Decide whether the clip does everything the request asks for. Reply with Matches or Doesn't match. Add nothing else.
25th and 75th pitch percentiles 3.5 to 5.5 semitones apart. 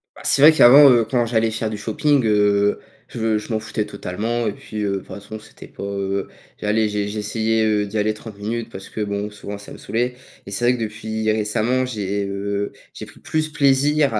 Doesn't match